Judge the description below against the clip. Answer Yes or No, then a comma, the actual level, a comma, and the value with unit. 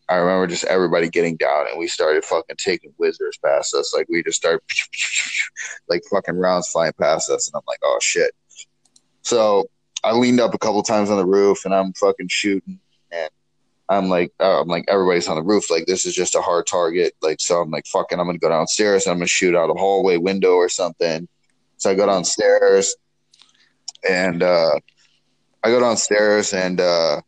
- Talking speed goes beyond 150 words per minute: Yes, average, 200 wpm